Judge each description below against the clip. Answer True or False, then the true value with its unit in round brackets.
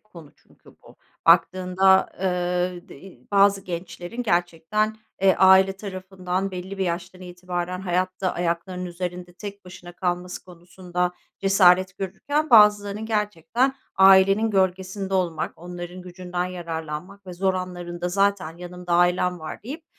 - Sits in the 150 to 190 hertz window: True (185 Hz)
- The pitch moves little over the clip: True (1.6 semitones)